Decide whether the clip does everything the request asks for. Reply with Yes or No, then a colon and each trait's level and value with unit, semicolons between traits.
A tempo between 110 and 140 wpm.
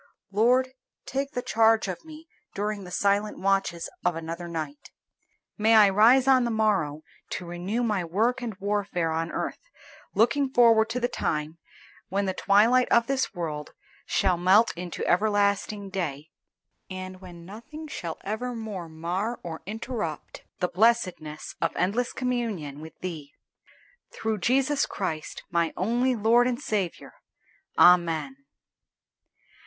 Yes: slow, 135 wpm